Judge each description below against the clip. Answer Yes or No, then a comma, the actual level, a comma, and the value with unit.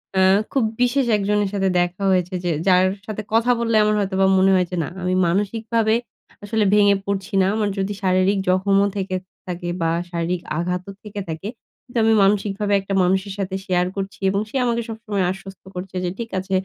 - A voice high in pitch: Yes, high, 195 Hz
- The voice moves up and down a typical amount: No, narrow, 2.1 semitones